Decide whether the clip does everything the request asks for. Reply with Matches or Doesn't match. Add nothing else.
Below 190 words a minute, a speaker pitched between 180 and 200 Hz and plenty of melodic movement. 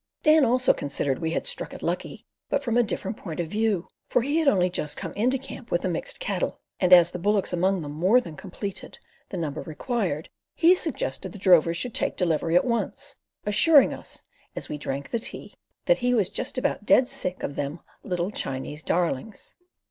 Doesn't match